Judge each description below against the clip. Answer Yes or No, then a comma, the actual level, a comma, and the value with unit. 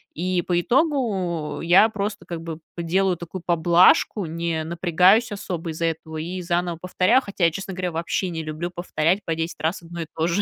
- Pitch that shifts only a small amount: Yes, narrow, 2.2 semitones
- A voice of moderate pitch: Yes, medium, 175 Hz